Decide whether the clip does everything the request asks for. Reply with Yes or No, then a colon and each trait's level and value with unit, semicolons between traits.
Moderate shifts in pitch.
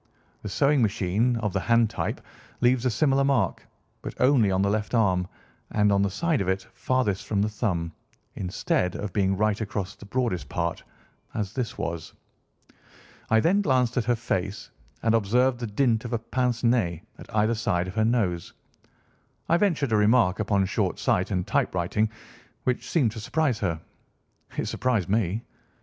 Yes: average, 4.2 semitones